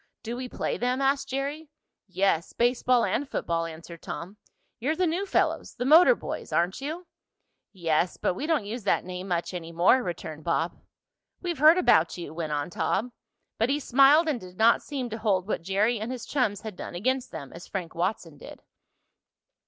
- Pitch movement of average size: No, wide, 7.7 semitones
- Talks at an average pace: Yes, average, 190 wpm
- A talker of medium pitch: No, high, 220 Hz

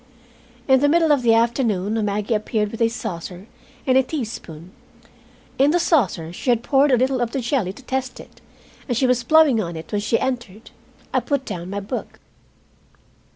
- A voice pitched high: Yes, high, 235 Hz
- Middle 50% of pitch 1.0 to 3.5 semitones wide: No, average, 4.3 semitones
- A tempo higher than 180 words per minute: Yes, average, 190 wpm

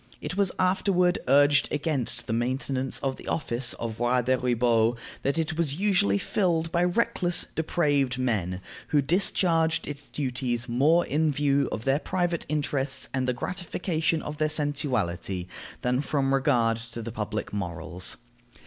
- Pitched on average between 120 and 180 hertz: Yes, medium, 140 Hz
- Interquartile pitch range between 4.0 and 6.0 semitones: Yes, average, 5.0 semitones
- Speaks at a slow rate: No, average, 150 wpm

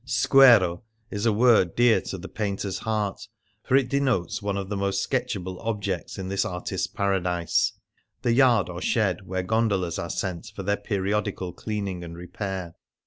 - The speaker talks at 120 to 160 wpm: No, average, 170 wpm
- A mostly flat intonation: No, average, 3.3 semitones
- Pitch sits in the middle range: No, low, 100 Hz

